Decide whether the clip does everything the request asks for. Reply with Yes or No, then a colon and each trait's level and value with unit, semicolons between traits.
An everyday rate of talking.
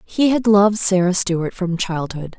Yes: average, 175 wpm